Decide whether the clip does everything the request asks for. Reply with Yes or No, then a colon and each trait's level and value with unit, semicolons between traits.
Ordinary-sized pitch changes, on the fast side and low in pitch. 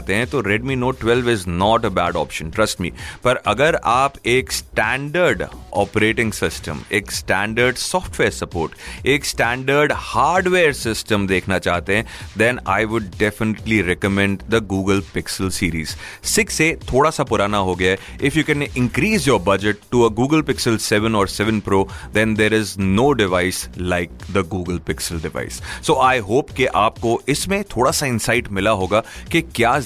No: average, 4.0 semitones; average, 165 wpm; low, 105 Hz